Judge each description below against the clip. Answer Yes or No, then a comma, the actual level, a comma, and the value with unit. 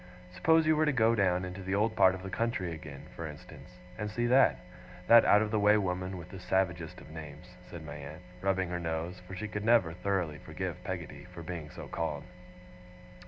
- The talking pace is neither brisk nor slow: No, fast, 210 wpm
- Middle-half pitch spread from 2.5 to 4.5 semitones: Yes, average, 4.0 semitones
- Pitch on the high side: No, very low, 90 Hz